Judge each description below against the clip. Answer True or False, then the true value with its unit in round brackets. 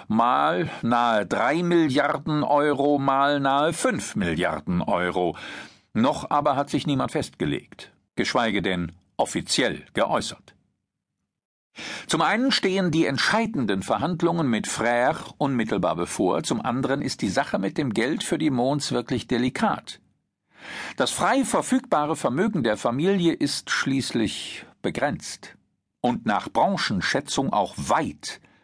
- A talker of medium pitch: True (145 Hz)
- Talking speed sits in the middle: False (120 wpm)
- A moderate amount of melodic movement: False (6.6 semitones)